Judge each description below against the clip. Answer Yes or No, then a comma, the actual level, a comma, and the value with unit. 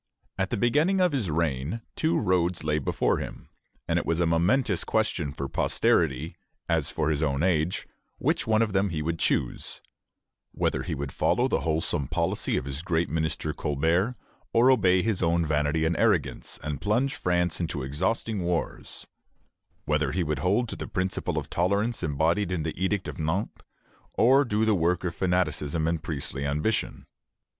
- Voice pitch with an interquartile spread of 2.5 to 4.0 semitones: No, average, 4.8 semitones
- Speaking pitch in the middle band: No, very low, 85 Hz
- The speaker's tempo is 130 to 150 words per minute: No, average, 175 wpm